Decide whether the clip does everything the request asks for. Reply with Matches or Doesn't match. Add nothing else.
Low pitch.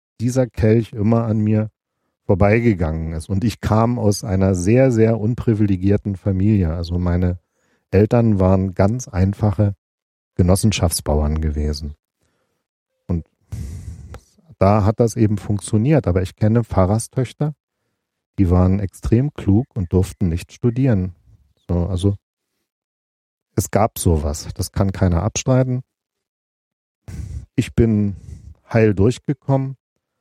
Matches